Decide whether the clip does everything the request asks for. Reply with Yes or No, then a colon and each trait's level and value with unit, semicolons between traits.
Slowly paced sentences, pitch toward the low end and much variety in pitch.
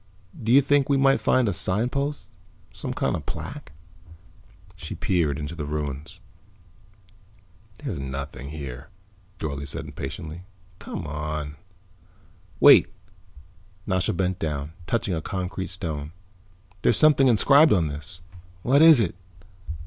Yes: slow, 125 wpm; very low, 85 Hz; wide, 7.8 semitones